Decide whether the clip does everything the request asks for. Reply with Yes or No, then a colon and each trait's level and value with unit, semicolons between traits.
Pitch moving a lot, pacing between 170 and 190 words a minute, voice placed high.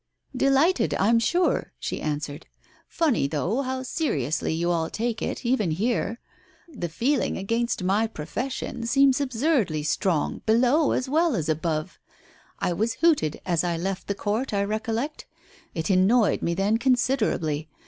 No: wide, 7.5 semitones; average, 145 wpm; high, 220 Hz